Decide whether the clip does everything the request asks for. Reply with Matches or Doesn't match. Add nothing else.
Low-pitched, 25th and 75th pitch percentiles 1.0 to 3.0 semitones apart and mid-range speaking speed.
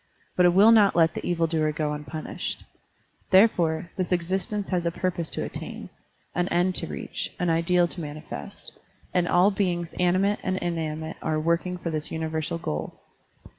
Doesn't match